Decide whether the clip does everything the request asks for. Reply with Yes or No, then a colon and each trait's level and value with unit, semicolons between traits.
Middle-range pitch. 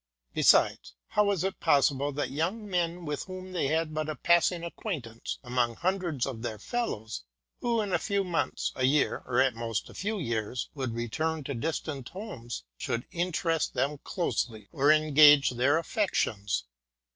Yes: medium, 150 Hz